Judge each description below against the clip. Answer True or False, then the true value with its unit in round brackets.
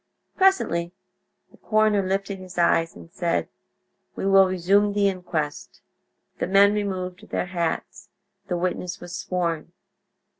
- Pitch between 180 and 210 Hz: True (185 Hz)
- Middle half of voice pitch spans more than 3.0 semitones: False (2.4 semitones)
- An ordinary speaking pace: False (125 wpm)